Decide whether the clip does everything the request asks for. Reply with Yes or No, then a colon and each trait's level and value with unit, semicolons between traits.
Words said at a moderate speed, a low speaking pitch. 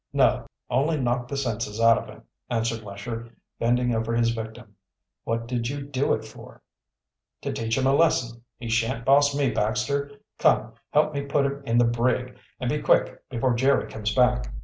Yes: average, 185 wpm; low, 120 Hz